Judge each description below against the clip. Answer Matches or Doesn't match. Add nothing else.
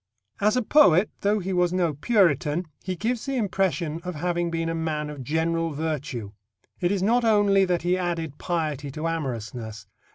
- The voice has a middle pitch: Matches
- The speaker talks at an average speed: Matches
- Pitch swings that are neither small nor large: Matches